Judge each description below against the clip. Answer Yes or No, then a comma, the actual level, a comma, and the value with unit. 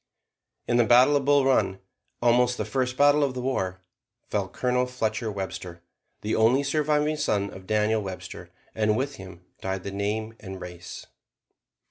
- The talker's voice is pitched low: Yes, low, 110 Hz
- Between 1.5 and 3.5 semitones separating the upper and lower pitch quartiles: No, average, 5.2 semitones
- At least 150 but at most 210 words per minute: Yes, average, 160 wpm